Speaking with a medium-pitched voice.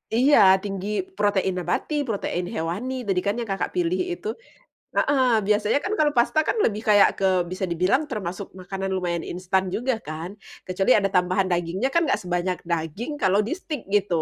No: high, 195 Hz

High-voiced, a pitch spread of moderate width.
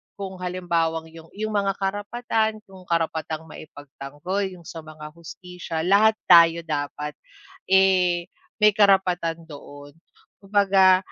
No: medium, 180 Hz; average, 3.3 semitones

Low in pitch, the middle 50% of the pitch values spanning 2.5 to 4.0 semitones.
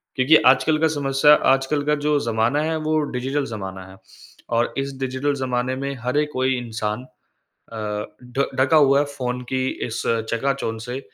Yes: low, 130 Hz; average, 3.4 semitones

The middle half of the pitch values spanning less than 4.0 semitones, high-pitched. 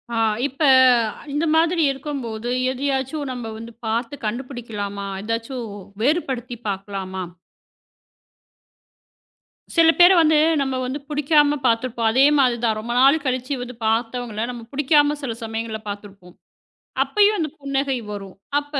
No: average, 4.3 semitones; very high, 250 Hz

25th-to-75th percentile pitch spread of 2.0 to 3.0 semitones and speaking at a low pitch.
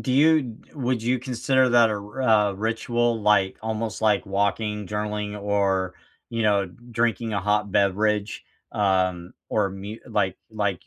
Yes: narrow, 2.5 semitones; low, 105 Hz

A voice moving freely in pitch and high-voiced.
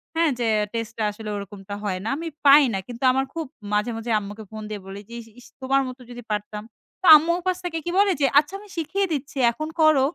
Yes: wide, 6.7 semitones; very high, 255 Hz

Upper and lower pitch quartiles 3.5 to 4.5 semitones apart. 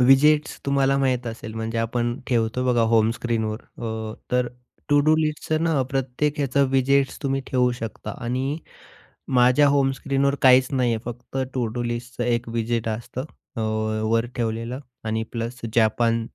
No: average, 2.8 semitones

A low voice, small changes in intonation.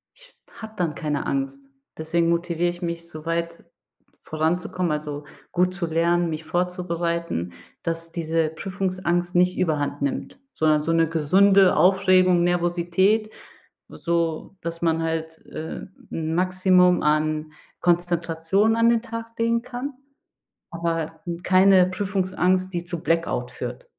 No: medium, 175 Hz; narrow, 2.3 semitones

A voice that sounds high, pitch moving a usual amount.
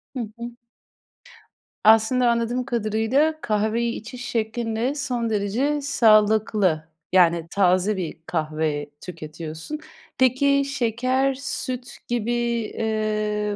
Yes: high, 225 Hz; average, 3.8 semitones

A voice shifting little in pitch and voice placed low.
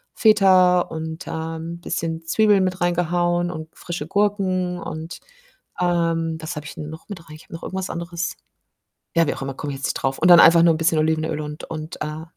No: narrow, 2.0 semitones; medium, 165 Hz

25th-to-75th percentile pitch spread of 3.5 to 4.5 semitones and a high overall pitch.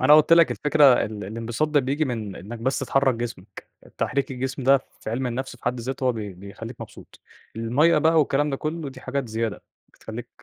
No: average, 3.8 semitones; low, 130 Hz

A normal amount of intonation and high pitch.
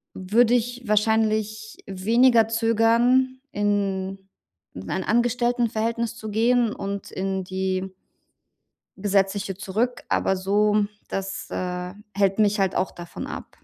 Yes: average, 3.2 semitones; high, 210 Hz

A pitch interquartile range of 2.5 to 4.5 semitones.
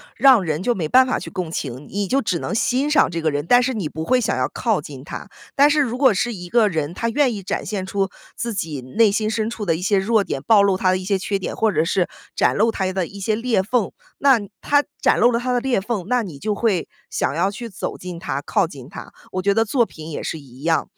No: average, 5.0 semitones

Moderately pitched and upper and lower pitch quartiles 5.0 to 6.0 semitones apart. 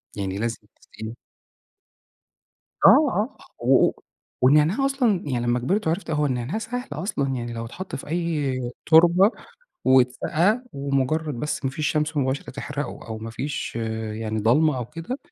Yes: medium, 145 Hz; average, 5.3 semitones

